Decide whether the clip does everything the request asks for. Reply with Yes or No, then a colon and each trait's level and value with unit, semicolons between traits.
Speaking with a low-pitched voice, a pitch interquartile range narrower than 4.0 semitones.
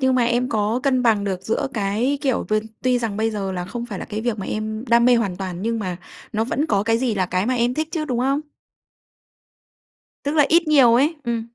No: high, 235 Hz; average, 3.5 semitones